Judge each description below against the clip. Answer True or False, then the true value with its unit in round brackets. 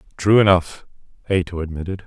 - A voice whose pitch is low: True (90 Hz)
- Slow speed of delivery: True (115 wpm)